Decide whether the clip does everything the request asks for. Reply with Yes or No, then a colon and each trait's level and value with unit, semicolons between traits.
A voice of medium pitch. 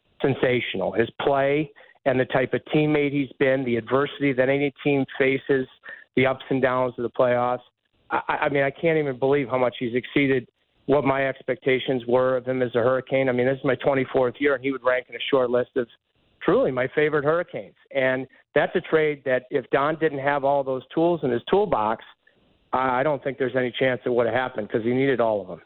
No: low, 130 Hz